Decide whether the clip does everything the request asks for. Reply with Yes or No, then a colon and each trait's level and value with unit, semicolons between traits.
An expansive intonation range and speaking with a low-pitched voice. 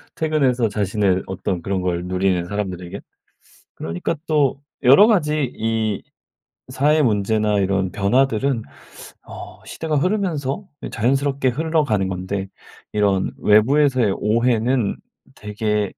Yes: wide, 6.0 semitones; low, 110 Hz